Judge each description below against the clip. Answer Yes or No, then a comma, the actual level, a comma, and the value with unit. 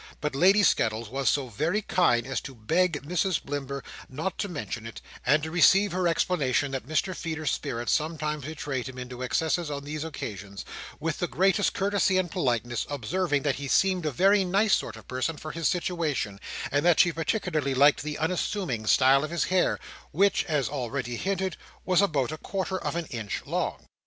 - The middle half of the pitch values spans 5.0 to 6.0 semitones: Yes, wide, 5.4 semitones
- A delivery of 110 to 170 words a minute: No, average, 185 wpm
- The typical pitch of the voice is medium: Yes, medium, 155 Hz